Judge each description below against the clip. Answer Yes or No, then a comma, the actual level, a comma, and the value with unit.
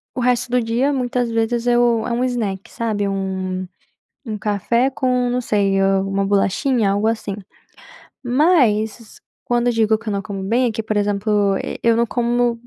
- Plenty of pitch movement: No, average, 3.2 semitones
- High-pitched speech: Yes, high, 225 Hz